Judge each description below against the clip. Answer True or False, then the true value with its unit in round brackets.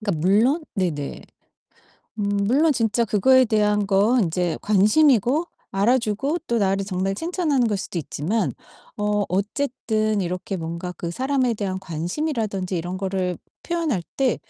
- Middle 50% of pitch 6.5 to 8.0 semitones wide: False (5.2 semitones)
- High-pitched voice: True (210 Hz)